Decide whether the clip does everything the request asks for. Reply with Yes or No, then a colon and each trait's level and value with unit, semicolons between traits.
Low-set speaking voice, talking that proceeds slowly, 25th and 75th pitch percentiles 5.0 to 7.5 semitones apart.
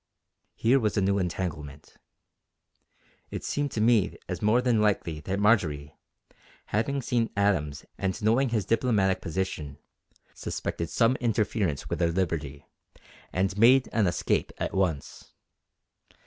Yes: low, 100 Hz; slow, 130 wpm; average, 5.3 semitones